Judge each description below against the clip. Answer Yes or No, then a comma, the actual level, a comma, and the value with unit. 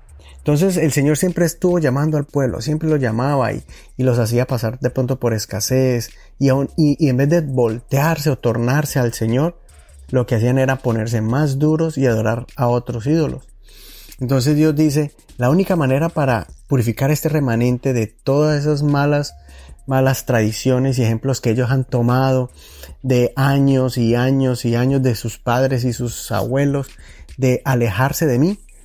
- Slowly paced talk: No, average, 170 wpm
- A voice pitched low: Yes, low, 130 Hz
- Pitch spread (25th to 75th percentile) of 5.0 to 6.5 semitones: No, average, 3.4 semitones